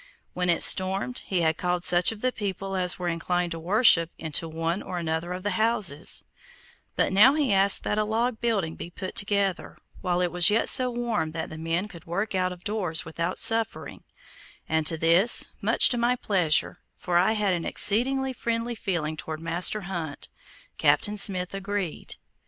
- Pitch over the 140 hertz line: Yes, medium, 185 Hz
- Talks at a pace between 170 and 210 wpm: Yes, average, 185 wpm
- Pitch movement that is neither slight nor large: Yes, average, 4.1 semitones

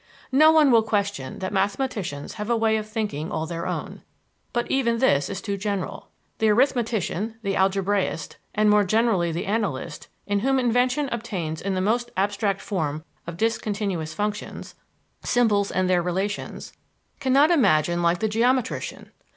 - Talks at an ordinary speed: Yes, average, 155 wpm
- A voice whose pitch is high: Yes, high, 205 Hz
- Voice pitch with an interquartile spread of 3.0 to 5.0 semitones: Yes, average, 3.9 semitones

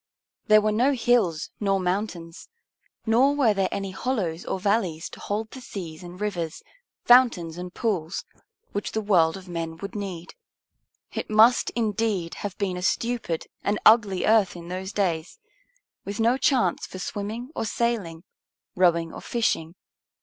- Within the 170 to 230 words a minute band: No, average, 155 wpm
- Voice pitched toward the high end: Yes, high, 200 Hz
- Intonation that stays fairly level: No, average, 4.2 semitones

